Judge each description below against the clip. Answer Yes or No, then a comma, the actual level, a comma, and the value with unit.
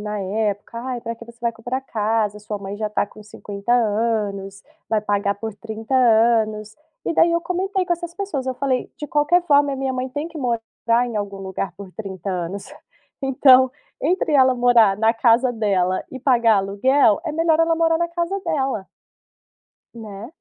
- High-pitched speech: Yes, high, 230 Hz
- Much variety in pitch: No, average, 4.5 semitones